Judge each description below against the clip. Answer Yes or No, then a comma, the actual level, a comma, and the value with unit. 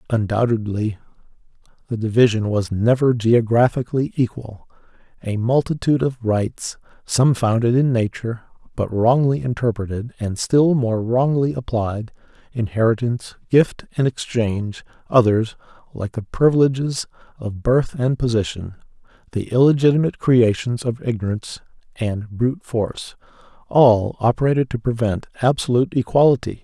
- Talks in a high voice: No, low, 120 Hz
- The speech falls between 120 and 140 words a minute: No, slow, 110 wpm